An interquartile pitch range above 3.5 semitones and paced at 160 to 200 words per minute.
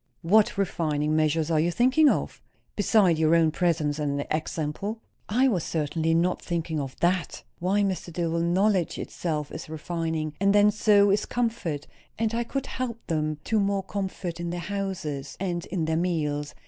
Yes: average, 4.3 semitones; average, 170 wpm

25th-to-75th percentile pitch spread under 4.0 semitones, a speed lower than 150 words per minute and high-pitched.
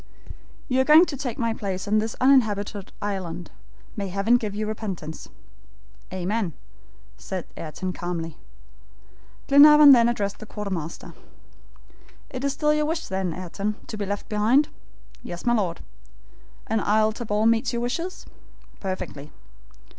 No: average, 4.4 semitones; average, 140 wpm; high, 210 Hz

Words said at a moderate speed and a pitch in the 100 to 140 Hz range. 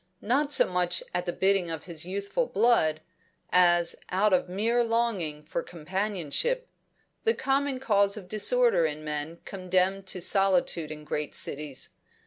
No: average, 145 wpm; medium, 185 Hz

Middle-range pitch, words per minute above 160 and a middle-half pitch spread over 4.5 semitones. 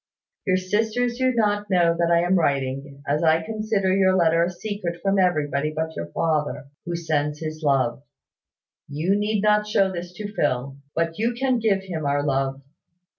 Yes: medium, 170 Hz; average, 175 wpm; wide, 5.5 semitones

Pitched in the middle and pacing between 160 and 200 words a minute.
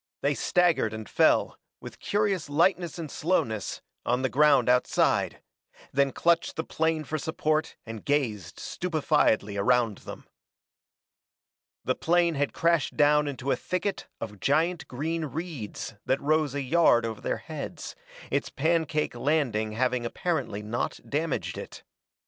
No: medium, 145 Hz; slow, 135 wpm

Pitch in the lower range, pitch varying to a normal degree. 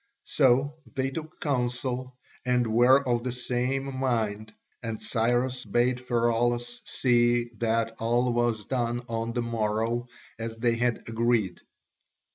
No: low, 120 Hz; narrow, 1.5 semitones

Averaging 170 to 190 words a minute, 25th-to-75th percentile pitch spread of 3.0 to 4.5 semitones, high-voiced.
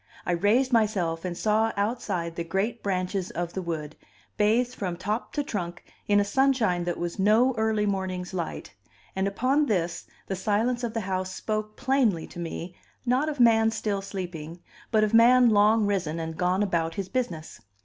Yes: average, 180 wpm; average, 4.1 semitones; high, 200 Hz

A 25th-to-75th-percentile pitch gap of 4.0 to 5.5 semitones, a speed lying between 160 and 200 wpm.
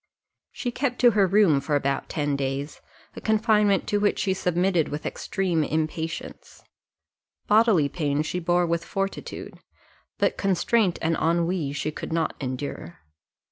No: average, 4.8 semitones; average, 140 wpm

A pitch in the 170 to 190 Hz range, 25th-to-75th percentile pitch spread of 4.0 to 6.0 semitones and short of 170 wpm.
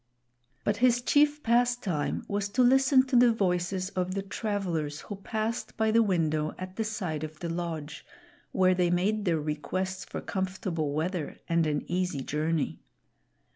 Yes: medium, 185 Hz; average, 5.0 semitones; average, 160 wpm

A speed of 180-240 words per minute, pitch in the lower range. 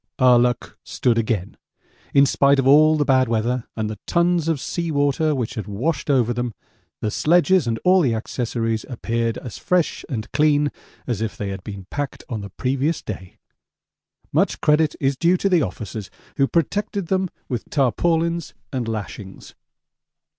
No: average, 170 wpm; low, 130 Hz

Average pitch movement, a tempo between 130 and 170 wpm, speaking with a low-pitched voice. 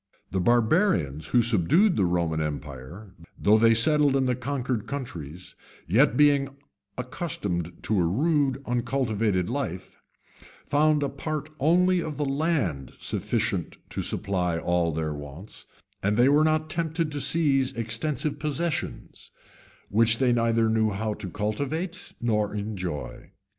No: wide, 7.7 semitones; slow, 135 wpm; low, 120 Hz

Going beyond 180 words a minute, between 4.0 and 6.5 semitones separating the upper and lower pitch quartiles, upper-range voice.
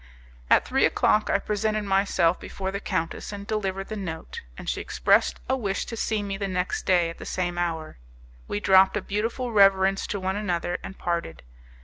No: average, 195 wpm; average, 2.8 semitones; high, 195 Hz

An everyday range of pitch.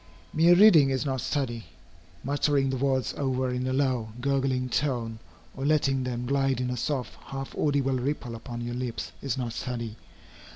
No: narrow, 2.1 semitones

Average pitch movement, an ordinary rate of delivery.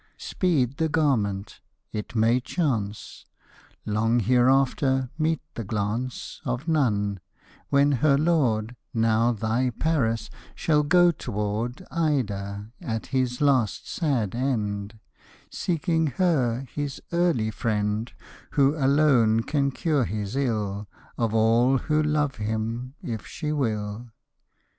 No: average, 4.9 semitones; slow, 115 wpm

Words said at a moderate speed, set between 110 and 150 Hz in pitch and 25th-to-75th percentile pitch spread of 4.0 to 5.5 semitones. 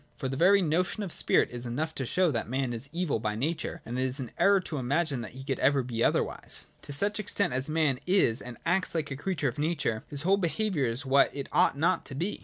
No: fast, 255 wpm; medium, 140 Hz; average, 5.2 semitones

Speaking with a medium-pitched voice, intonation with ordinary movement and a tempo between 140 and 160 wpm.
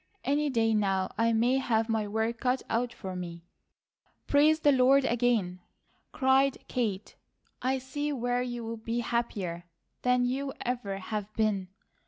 No: high, 235 Hz; average, 3.4 semitones; average, 150 wpm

